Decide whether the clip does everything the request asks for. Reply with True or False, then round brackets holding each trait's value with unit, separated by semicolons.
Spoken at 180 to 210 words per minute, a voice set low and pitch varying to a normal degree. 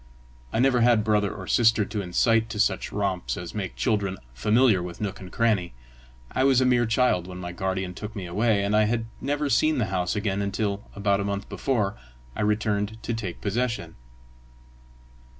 True (185 wpm; 105 Hz; 3.2 semitones)